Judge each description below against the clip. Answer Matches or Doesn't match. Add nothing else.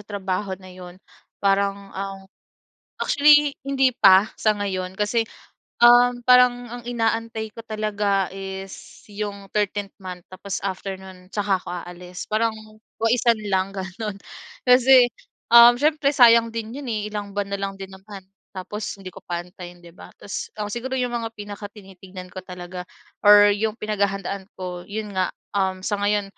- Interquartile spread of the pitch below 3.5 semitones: Matches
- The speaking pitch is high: Matches